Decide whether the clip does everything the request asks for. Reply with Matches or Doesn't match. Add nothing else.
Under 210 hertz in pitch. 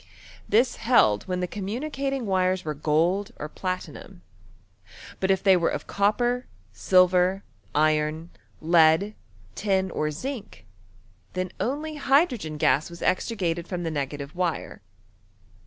Matches